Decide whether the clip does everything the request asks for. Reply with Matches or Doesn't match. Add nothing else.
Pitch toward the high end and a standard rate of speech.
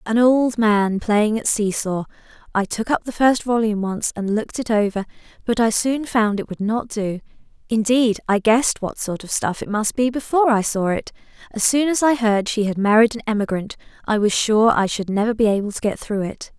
Doesn't match